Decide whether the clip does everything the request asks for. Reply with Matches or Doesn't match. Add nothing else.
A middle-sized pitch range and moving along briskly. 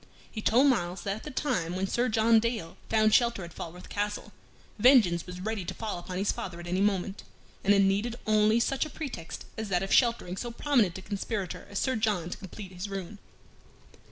Matches